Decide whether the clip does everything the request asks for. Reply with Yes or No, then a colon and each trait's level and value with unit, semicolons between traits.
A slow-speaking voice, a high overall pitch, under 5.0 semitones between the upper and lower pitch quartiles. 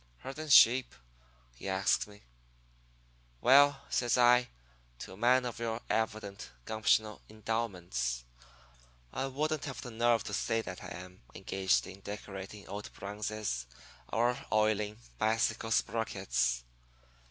No: slow, 120 wpm; low, 110 Hz; average, 3.6 semitones